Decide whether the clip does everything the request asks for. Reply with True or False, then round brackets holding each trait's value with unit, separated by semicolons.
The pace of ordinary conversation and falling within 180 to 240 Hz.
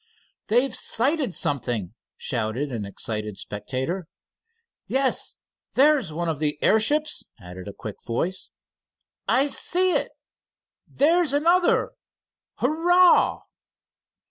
False (95 wpm; 190 Hz)